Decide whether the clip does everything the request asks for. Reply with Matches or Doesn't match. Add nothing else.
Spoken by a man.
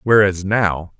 Matches